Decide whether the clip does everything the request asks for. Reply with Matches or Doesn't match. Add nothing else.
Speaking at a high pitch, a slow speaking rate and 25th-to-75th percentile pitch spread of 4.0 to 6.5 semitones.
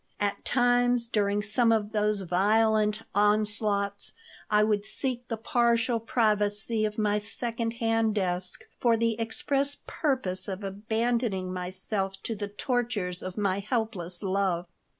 Doesn't match